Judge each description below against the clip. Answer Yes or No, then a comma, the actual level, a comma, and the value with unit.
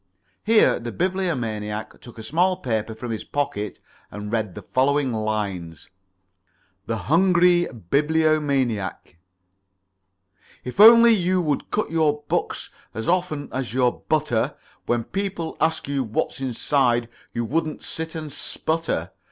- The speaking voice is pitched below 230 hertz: Yes, medium, 140 Hz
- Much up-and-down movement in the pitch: Yes, wide, 6.6 semitones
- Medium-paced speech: No, slow, 125 wpm